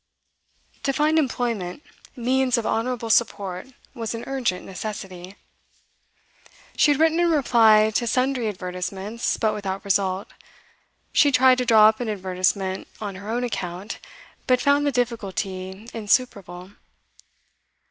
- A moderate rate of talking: No, slow, 125 wpm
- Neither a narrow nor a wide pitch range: Yes, average, 4.7 semitones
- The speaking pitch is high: Yes, high, 220 Hz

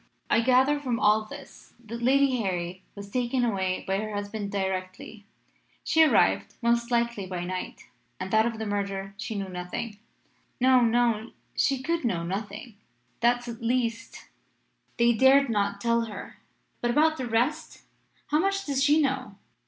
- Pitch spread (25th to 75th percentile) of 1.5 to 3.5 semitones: No, average, 4.1 semitones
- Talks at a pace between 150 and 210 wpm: Yes, average, 160 wpm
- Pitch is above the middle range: Yes, high, 230 Hz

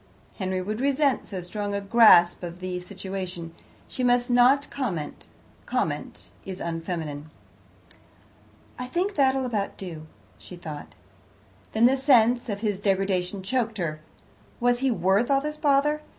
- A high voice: Yes, high, 205 Hz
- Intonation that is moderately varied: No, wide, 5.8 semitones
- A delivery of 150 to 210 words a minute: No, average, 140 wpm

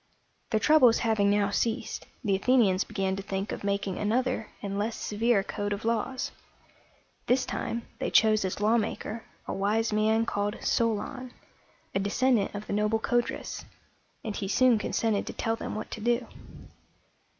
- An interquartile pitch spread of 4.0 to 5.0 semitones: No, narrow, 2.4 semitones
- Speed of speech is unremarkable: Yes, average, 160 wpm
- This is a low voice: No, high, 215 Hz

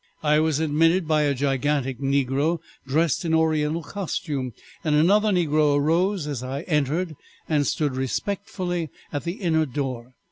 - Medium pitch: Yes, medium, 150 Hz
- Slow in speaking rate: No, average, 145 wpm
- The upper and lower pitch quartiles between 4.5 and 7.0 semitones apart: No, average, 3.0 semitones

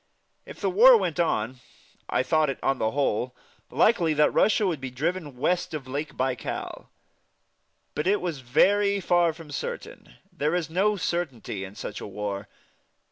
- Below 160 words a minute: No, average, 165 wpm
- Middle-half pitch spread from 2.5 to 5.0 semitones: No, wide, 5.6 semitones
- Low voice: No, medium, 150 Hz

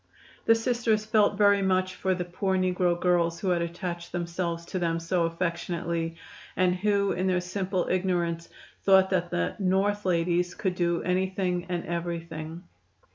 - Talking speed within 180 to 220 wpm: No, average, 155 wpm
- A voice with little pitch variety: Yes, narrow, 1.8 semitones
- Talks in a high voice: No, medium, 180 Hz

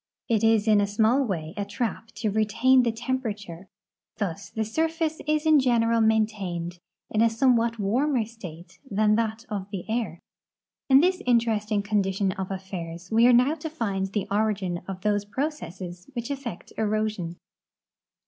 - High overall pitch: Yes, high, 215 Hz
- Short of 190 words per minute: Yes, average, 170 wpm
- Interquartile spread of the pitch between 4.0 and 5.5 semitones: No, average, 3.4 semitones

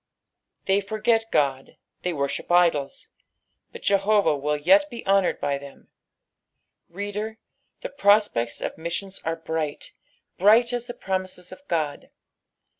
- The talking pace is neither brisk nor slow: No, slow, 125 wpm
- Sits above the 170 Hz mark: Yes, medium, 185 Hz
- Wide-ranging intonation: Yes, wide, 5.7 semitones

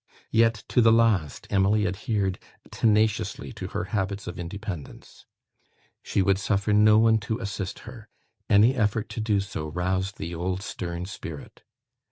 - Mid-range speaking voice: No, low, 100 Hz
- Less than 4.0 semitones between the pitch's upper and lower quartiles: Yes, average, 2.8 semitones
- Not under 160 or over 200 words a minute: No, average, 150 wpm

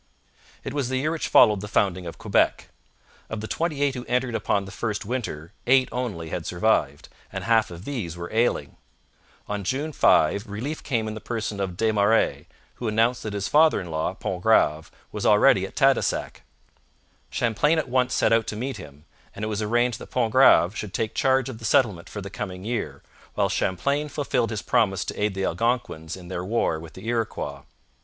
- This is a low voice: Yes, low, 110 Hz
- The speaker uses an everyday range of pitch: Yes, average, 4.5 semitones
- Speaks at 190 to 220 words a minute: Yes, average, 195 wpm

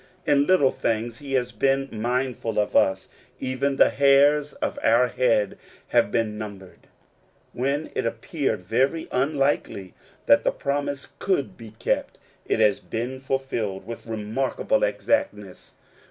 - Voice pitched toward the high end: No, low, 125 Hz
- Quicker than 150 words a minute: No, slow, 135 wpm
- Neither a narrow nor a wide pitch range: Yes, average, 3.9 semitones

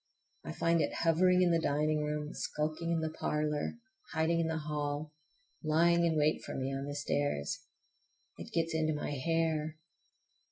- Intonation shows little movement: Yes, narrow, 1.7 semitones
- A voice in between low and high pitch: Yes, medium, 155 Hz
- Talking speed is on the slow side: No, average, 165 wpm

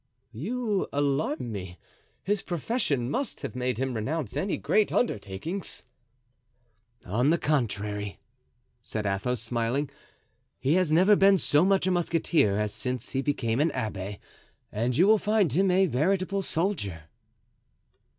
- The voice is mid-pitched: Yes, medium, 145 Hz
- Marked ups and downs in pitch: Yes, wide, 8.6 semitones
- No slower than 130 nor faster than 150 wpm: Yes, slow, 135 wpm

